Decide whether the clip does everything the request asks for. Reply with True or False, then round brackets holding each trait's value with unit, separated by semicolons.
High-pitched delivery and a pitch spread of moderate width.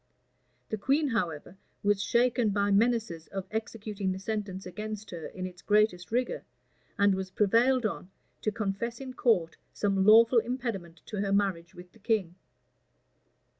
True (205 Hz; 3.2 semitones)